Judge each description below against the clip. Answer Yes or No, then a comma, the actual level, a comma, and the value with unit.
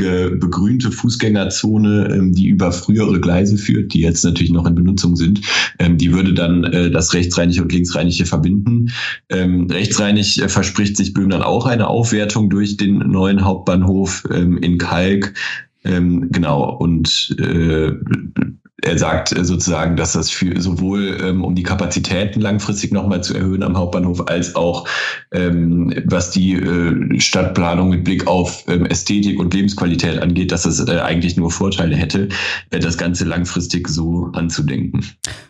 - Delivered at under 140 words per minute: Yes, average, 130 wpm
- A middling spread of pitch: No, narrow, 2.1 semitones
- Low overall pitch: Yes, very low, 90 Hz